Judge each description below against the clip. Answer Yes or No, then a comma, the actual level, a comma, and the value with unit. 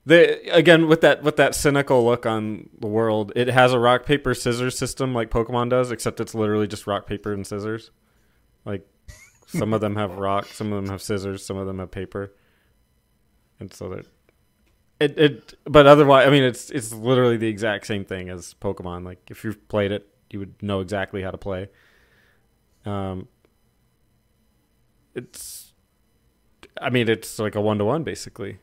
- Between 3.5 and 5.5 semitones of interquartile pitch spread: Yes, average, 4.0 semitones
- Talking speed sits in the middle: Yes, average, 180 wpm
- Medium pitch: No, low, 110 Hz